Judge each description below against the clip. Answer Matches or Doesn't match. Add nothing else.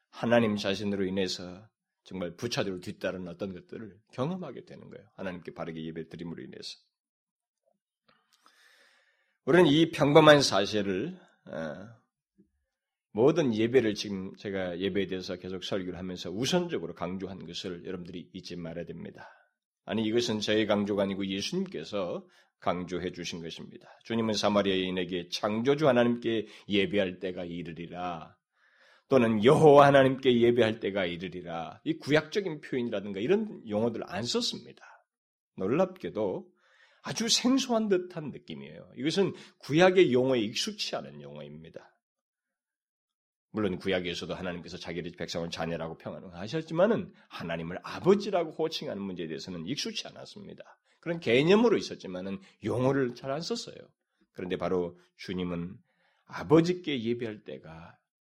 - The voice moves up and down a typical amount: Doesn't match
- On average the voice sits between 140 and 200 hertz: Doesn't match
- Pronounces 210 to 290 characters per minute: Doesn't match